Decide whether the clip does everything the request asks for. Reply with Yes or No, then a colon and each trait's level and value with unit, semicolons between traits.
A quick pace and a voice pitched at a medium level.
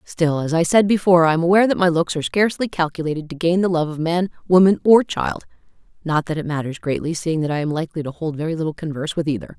Yes: fast, 250 wpm; medium, 160 Hz